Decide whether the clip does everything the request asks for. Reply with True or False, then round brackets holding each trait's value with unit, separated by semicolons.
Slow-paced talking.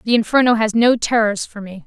False (225 wpm)